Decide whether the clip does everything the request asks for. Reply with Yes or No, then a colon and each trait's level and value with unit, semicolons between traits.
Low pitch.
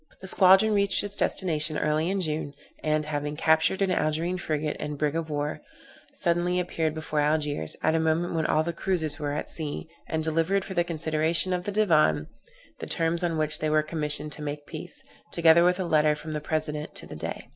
No: medium, 160 Hz